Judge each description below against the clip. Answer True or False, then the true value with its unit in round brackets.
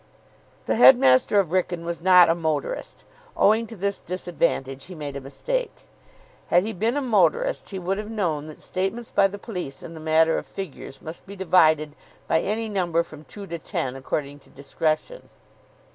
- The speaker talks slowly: False (180 wpm)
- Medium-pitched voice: True (180 Hz)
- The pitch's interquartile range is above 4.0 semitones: True (4.7 semitones)